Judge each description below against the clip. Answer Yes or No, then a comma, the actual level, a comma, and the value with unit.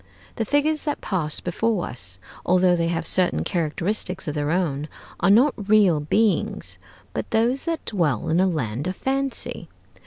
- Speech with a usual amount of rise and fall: No, wide, 5.7 semitones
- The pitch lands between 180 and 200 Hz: Yes, medium, 185 Hz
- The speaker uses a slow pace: No, average, 160 wpm